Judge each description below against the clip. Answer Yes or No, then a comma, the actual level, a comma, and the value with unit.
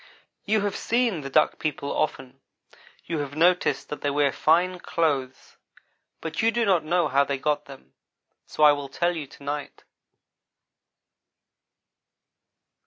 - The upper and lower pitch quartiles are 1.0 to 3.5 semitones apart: No, average, 3.9 semitones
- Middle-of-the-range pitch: Yes, medium, 150 Hz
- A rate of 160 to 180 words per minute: No, average, 145 wpm